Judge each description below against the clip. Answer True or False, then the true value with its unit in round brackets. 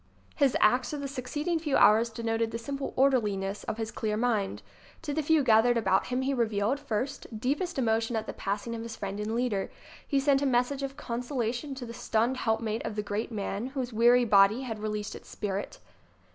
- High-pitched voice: True (235 Hz)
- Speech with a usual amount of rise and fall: True (3.7 semitones)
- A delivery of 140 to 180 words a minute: False (205 wpm)